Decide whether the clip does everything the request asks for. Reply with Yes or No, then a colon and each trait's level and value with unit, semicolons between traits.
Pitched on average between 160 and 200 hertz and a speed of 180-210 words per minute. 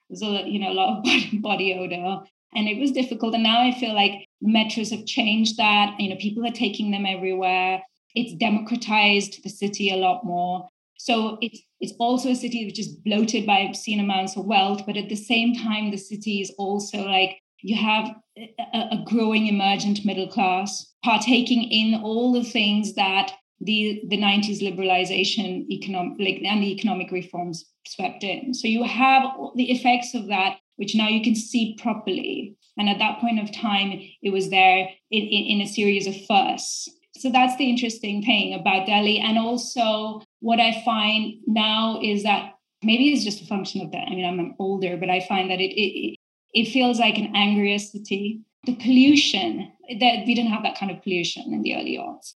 No: high, 215 Hz; average, 190 wpm